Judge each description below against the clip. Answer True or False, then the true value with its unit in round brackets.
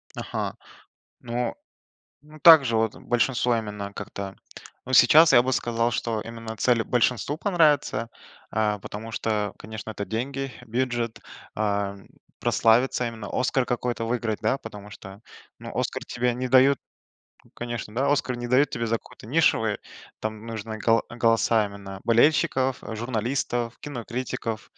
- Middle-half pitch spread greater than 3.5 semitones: False (2.6 semitones)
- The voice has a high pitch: False (115 Hz)